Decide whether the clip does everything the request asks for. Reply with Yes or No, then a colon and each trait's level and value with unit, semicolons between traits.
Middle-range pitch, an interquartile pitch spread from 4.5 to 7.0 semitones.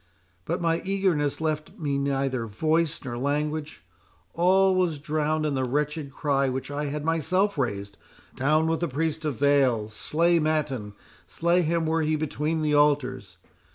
No: medium, 150 Hz; average, 3.1 semitones